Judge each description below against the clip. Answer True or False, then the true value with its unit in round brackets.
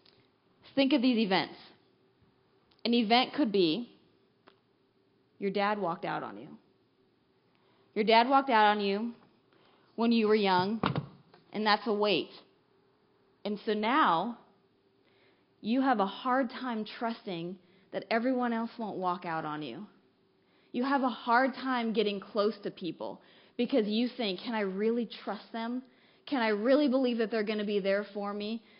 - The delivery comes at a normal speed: True (155 wpm)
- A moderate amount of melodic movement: True (3.2 semitones)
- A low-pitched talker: False (220 Hz)